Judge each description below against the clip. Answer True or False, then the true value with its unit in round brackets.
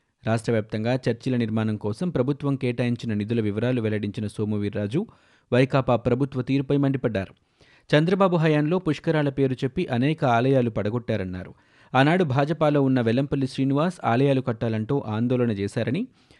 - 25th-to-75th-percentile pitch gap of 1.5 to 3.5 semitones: False (3.9 semitones)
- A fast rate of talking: False (115 wpm)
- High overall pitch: False (125 Hz)